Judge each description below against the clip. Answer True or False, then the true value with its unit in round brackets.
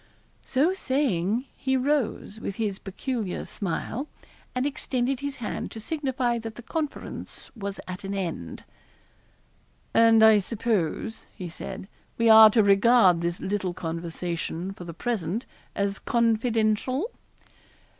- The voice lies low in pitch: False (220 Hz)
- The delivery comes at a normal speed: False (125 wpm)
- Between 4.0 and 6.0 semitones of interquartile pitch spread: True (4.6 semitones)